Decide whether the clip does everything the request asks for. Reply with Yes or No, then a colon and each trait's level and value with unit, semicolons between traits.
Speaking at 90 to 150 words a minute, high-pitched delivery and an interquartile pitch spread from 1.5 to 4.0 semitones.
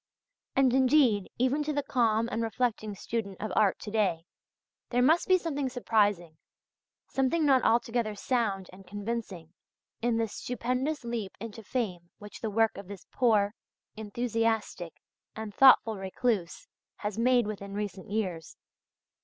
Yes: average, 140 wpm; high, 225 Hz; average, 3.6 semitones